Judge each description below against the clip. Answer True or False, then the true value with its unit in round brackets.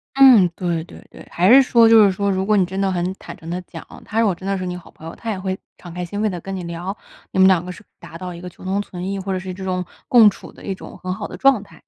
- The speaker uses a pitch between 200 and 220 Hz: False (190 Hz)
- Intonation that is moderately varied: False (2.2 semitones)